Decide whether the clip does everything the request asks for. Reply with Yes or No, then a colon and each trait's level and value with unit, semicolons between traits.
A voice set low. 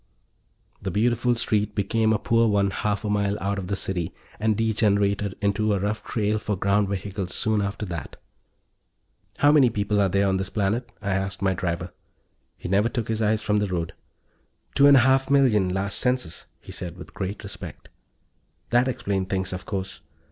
Yes: low, 100 Hz